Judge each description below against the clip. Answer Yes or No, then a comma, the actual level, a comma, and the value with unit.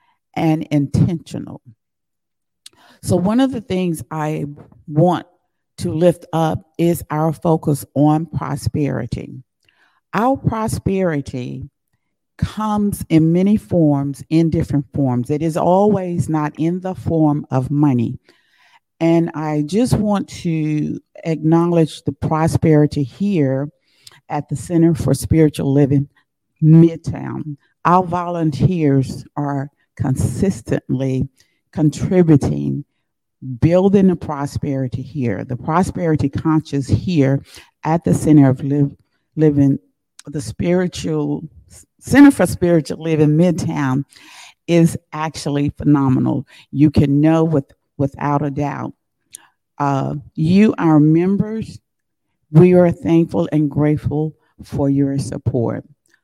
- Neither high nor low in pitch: Yes, medium, 150 Hz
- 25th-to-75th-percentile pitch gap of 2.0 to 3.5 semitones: Yes, average, 3.1 semitones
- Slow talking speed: Yes, slow, 105 wpm